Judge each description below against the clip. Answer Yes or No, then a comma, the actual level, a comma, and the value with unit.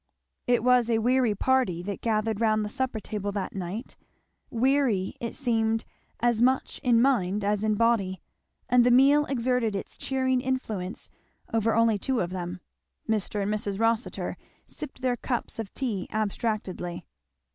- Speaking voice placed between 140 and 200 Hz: No, high, 225 Hz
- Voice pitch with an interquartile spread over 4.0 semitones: No, average, 3.5 semitones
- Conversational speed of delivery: Yes, average, 155 wpm